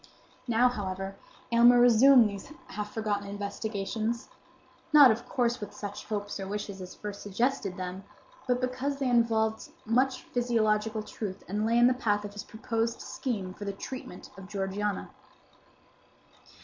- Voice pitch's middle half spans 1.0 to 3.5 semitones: Yes, average, 3.1 semitones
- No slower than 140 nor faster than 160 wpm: Yes, average, 150 wpm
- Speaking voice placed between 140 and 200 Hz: No, high, 215 Hz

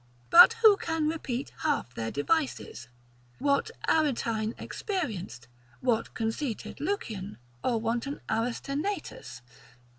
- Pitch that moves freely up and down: Yes, wide, 6.1 semitones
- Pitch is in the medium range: No, very high, 255 Hz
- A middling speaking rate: No, slow, 95 wpm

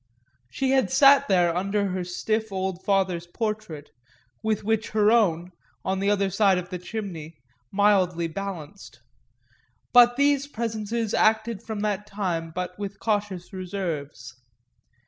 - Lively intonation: No, average, 3.3 semitones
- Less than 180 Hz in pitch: No, high, 200 Hz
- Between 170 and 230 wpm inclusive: No, slow, 135 wpm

